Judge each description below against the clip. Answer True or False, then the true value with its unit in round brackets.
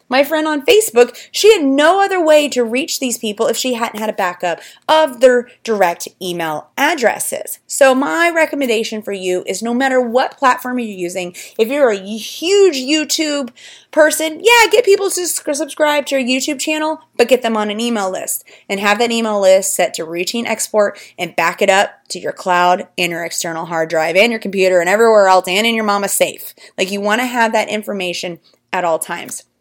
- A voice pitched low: False (230 Hz)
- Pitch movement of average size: False (7.8 semitones)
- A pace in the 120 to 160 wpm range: False (205 wpm)